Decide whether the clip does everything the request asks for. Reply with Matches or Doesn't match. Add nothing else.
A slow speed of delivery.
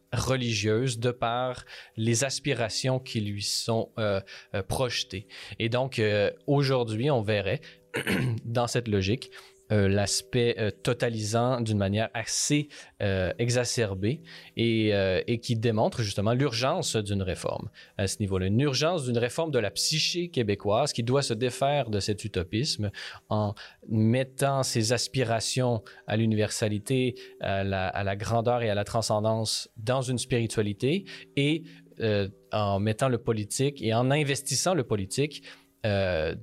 Matches